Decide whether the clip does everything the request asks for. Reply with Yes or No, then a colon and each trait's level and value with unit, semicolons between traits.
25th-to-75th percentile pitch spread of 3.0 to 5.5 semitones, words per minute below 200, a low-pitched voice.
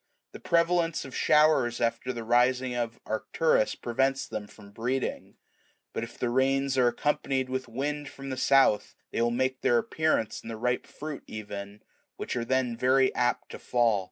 No: narrow, 2.6 semitones; average, 175 wpm; low, 125 Hz